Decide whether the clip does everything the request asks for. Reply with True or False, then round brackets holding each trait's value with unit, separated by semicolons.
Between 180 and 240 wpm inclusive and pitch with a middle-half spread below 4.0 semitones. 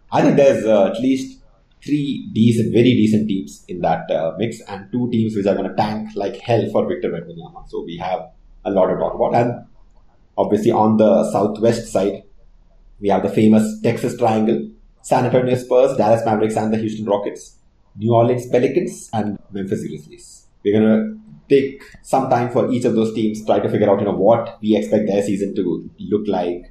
True (200 wpm; 2.6 semitones)